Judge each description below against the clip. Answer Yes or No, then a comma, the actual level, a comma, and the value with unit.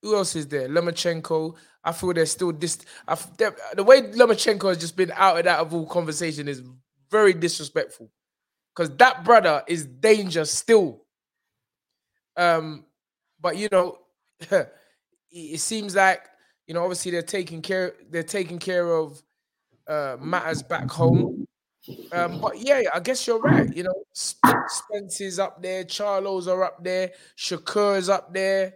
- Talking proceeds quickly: No, average, 150 wpm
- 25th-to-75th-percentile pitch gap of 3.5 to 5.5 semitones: No, average, 3.1 semitones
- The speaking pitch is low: No, medium, 180 Hz